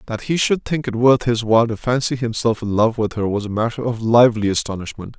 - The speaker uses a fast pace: Yes, fast, 245 wpm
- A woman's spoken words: No, male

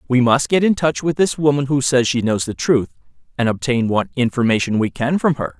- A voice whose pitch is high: No, low, 130 Hz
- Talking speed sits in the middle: No, fast, 235 wpm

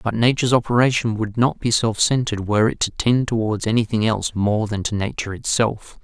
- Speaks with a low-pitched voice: Yes, low, 110 Hz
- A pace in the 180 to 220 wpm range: Yes, average, 200 wpm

